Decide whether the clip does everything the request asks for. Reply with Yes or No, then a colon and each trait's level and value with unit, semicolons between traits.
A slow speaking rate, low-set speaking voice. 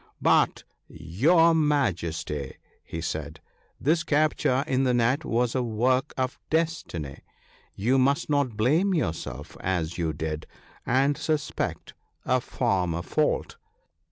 Yes: slow, 130 wpm; low, 125 Hz